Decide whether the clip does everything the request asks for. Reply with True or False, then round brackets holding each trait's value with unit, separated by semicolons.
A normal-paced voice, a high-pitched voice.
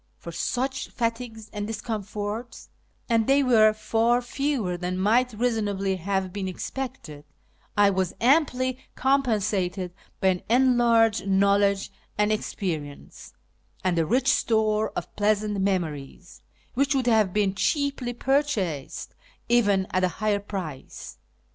False (125 wpm; 210 Hz)